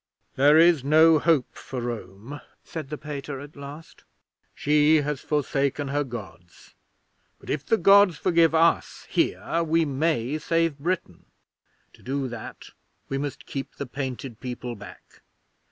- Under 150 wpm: Yes, average, 140 wpm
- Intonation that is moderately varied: Yes, average, 3.3 semitones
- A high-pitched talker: No, medium, 145 Hz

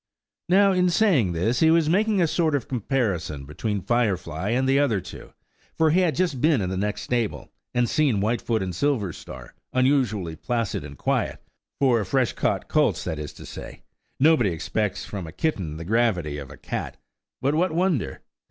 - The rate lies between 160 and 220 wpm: Yes, average, 180 wpm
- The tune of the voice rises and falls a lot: Yes, wide, 8.4 semitones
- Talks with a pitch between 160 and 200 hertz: No, low, 120 Hz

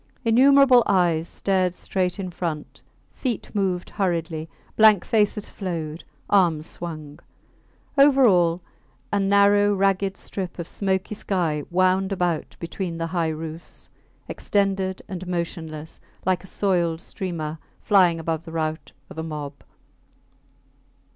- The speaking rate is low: Yes, slow, 120 wpm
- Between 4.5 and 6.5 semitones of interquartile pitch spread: No, average, 3.2 semitones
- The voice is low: No, medium, 180 Hz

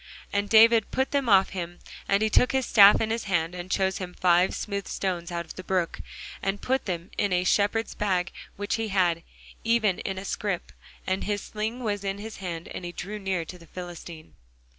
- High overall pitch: Yes, high, 195 Hz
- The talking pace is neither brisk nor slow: No, fast, 210 wpm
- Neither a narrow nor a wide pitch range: Yes, average, 3.0 semitones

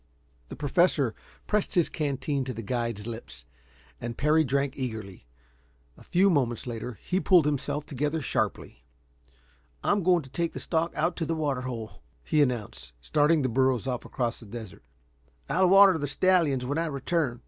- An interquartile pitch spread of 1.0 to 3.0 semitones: No, average, 5.3 semitones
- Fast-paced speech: No, average, 170 wpm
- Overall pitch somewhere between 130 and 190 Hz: Yes, medium, 140 Hz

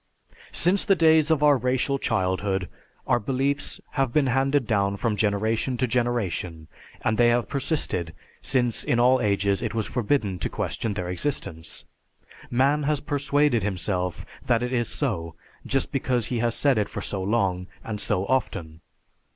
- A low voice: Yes, low, 120 Hz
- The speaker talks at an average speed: Yes, average, 160 wpm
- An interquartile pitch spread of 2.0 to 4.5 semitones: No, wide, 5.4 semitones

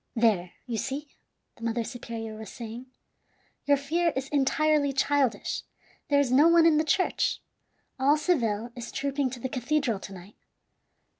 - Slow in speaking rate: No, average, 155 wpm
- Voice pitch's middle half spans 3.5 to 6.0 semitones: Yes, average, 4.1 semitones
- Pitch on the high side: Yes, very high, 265 Hz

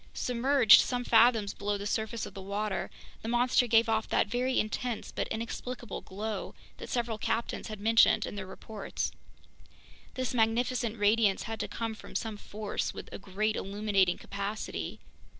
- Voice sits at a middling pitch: No, high, 220 Hz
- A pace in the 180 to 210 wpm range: No, average, 160 wpm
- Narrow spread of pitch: Yes, narrow, 2.3 semitones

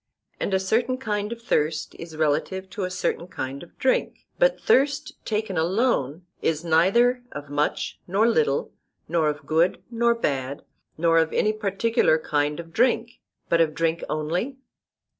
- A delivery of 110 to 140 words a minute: No, average, 160 wpm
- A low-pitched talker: No, medium, 175 Hz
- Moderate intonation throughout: No, wide, 6.6 semitones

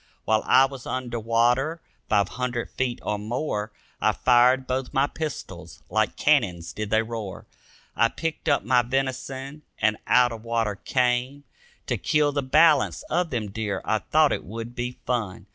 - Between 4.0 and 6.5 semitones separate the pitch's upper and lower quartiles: No, average, 3.1 semitones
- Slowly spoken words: No, average, 165 wpm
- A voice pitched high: No, low, 125 Hz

